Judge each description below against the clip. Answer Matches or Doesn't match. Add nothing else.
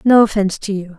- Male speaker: Doesn't match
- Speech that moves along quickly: Matches